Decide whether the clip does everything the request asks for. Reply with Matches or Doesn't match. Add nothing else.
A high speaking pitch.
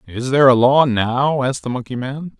Doesn't match